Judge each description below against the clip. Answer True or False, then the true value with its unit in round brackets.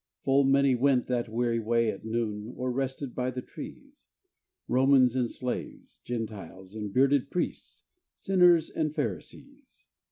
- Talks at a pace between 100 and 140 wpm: True (135 wpm)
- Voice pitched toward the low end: True (125 Hz)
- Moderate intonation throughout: True (3.1 semitones)